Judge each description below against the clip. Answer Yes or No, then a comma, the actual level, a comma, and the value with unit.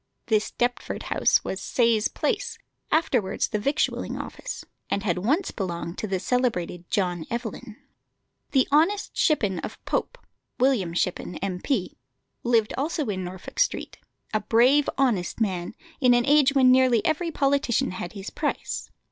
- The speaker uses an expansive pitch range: Yes, wide, 6.4 semitones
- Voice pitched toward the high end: Yes, high, 235 Hz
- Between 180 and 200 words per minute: No, average, 145 wpm